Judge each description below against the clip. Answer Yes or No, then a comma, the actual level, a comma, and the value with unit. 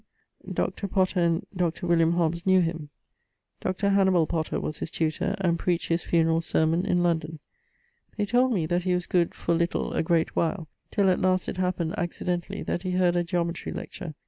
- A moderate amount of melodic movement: No, narrow, 1.7 semitones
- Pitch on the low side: No, medium, 175 Hz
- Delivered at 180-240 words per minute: Yes, average, 190 wpm